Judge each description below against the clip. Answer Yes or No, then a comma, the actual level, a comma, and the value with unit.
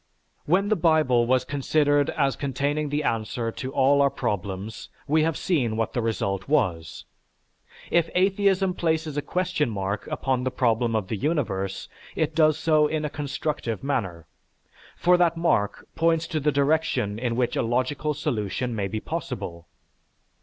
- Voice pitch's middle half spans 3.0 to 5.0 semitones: No, wide, 5.6 semitones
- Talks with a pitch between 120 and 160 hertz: Yes, medium, 140 Hz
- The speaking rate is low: No, average, 160 wpm